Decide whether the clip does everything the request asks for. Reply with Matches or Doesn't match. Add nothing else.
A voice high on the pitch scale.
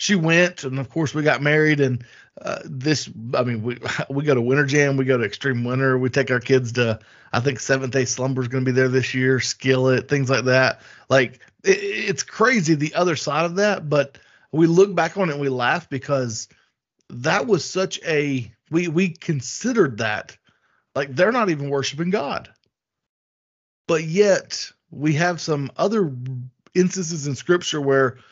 Doesn't match